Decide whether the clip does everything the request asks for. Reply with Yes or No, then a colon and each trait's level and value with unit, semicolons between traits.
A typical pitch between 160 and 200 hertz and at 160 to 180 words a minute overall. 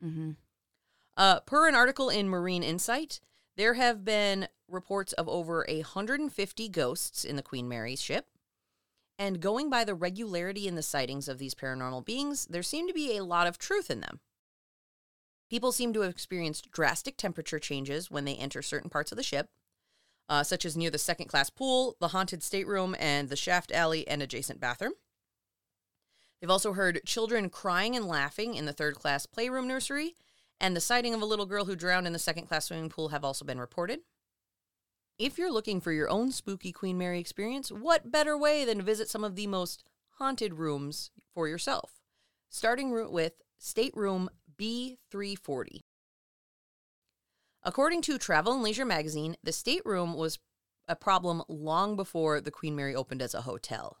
Yes: medium, 185 Hz; average, 175 wpm